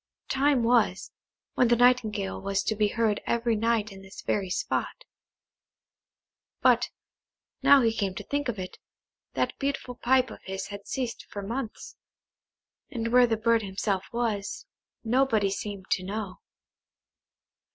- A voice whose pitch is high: Yes, high, 225 Hz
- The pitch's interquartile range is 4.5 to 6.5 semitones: No, average, 3.6 semitones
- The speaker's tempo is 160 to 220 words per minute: No, average, 140 wpm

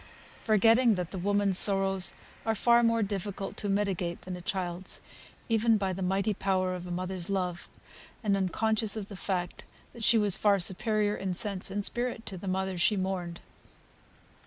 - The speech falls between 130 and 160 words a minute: No, average, 175 wpm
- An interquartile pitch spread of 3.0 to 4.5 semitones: No, narrow, 2.4 semitones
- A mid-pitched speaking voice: No, high, 195 Hz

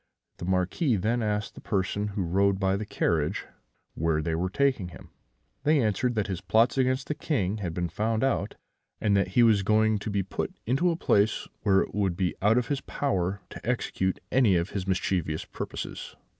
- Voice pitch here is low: Yes, low, 100 Hz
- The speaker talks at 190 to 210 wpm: Yes, average, 200 wpm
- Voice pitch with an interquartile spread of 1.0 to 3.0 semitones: No, average, 3.7 semitones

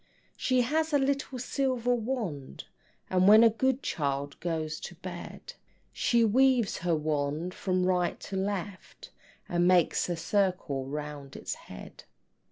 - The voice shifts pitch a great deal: Yes, wide, 7.6 semitones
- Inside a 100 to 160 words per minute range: Yes, average, 140 wpm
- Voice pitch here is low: No, medium, 185 Hz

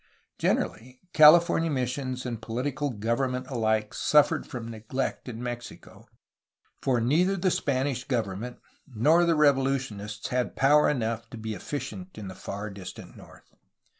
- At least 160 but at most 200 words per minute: No, slow, 135 wpm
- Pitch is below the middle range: Yes, low, 125 Hz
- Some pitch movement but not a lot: Yes, average, 4.2 semitones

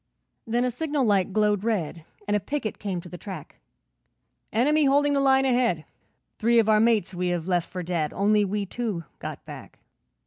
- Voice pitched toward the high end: Yes, high, 210 Hz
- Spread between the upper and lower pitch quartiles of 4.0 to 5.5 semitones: Yes, average, 5.1 semitones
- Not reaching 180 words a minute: No, average, 185 wpm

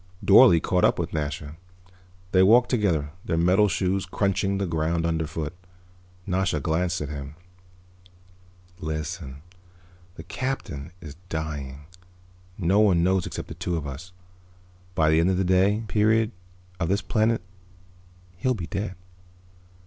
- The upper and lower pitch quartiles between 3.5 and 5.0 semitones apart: Yes, average, 3.9 semitones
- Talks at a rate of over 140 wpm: No, slow, 135 wpm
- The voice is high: No, very low, 90 Hz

